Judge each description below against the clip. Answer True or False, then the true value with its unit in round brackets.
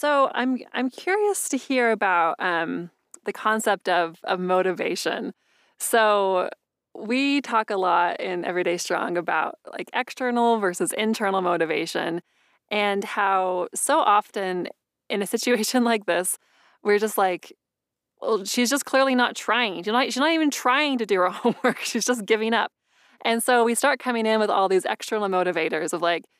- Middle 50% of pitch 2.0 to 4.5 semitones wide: False (5.0 semitones)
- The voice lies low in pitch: False (215 Hz)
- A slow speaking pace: False (165 wpm)